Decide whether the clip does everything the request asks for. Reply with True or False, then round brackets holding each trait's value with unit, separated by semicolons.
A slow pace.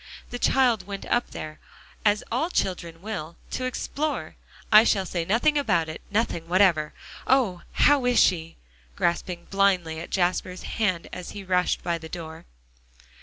False (150 wpm)